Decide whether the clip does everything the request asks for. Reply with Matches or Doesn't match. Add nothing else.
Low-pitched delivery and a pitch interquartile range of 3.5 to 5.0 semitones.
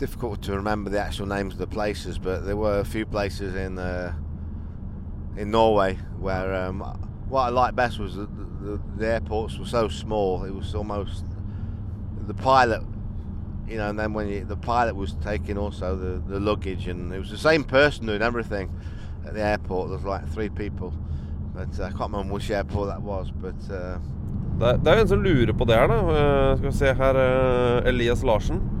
Doesn't match